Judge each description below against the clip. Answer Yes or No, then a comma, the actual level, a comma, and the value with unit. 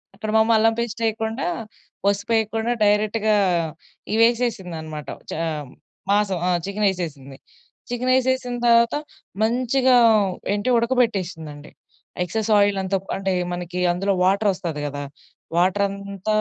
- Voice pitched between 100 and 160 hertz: No, high, 205 Hz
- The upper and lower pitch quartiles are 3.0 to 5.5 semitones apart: Yes, average, 3.7 semitones